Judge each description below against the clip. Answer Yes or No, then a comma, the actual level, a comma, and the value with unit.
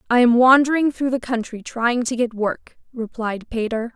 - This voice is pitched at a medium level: No, high, 240 Hz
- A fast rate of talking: No, average, 180 wpm